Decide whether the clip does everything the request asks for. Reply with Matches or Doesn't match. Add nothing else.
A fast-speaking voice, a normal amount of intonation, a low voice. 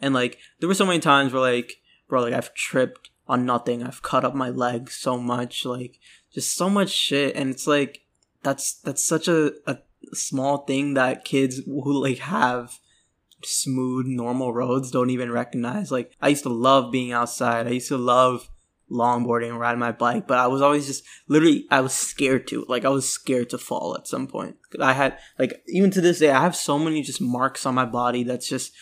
Doesn't match